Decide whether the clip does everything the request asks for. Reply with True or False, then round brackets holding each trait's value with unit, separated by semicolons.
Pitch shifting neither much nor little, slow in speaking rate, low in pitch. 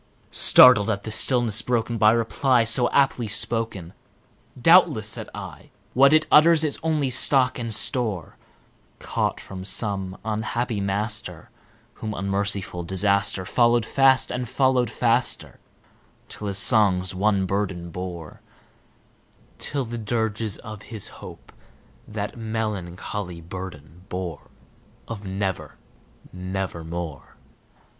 True (4.0 semitones; 115 wpm; 105 Hz)